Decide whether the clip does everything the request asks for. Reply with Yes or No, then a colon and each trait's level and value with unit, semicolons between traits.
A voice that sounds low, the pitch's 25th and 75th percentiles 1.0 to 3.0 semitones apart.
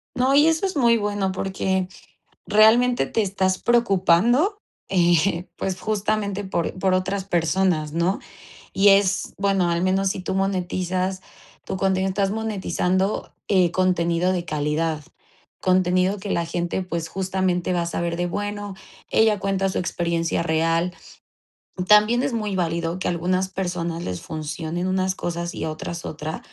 No: medium, 185 Hz; narrow, 2.5 semitones